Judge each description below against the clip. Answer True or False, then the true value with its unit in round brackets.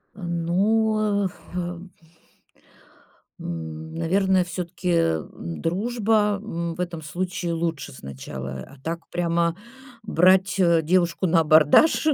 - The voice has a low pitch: False (170 Hz)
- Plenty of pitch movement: False (2.7 semitones)